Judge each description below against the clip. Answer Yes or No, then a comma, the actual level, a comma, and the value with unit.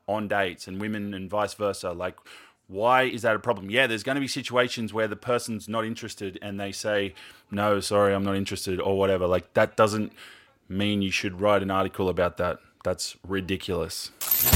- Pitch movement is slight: Yes, narrow, 2.2 semitones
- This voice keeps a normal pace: Yes, average, 190 wpm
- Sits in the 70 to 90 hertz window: No, low, 100 Hz